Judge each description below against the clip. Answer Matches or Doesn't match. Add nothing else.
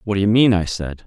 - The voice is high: Doesn't match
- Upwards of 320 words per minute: Matches